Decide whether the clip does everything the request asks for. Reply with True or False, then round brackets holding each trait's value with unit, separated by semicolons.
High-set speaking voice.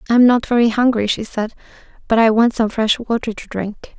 True (225 Hz)